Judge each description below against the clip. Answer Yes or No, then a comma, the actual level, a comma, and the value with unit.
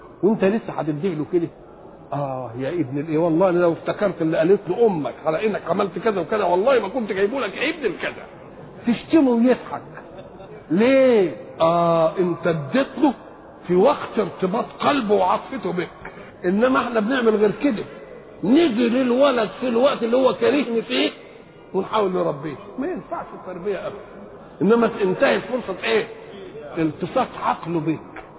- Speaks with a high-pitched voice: Yes, high, 200 Hz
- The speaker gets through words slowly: No, average, 140 wpm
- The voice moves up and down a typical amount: No, wide, 5.9 semitones